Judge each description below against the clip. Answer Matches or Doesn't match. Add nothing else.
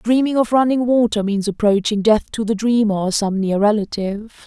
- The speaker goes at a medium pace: Matches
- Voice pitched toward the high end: Matches